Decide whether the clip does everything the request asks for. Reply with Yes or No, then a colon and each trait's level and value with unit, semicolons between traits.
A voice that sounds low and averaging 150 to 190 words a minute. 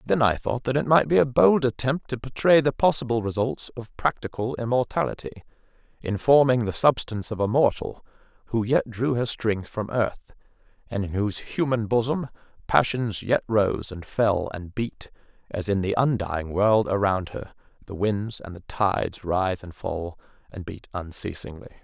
Yes: low, 110 Hz; average, 170 wpm